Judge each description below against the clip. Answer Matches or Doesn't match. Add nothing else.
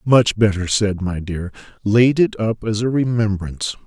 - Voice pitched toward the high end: Doesn't match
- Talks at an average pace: Matches